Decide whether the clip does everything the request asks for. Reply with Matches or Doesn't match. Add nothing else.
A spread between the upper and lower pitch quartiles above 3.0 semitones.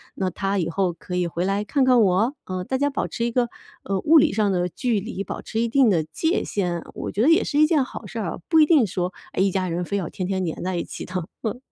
Matches